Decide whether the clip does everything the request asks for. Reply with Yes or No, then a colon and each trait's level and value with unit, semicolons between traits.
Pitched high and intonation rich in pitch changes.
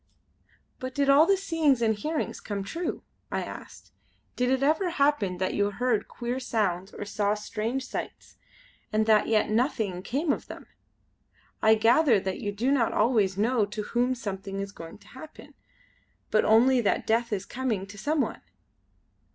No: high, 225 Hz; average, 4.4 semitones